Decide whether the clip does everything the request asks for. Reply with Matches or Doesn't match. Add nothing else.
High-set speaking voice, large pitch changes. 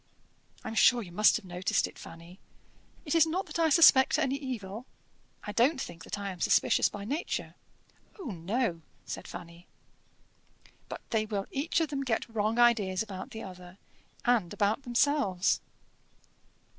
Matches